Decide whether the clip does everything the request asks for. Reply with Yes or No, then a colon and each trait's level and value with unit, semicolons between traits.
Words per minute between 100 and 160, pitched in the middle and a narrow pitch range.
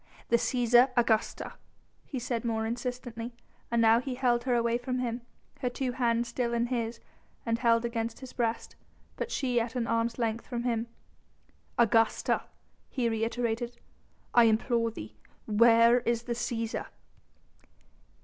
No: average, 145 wpm; high, 235 Hz; narrow, 1.1 semitones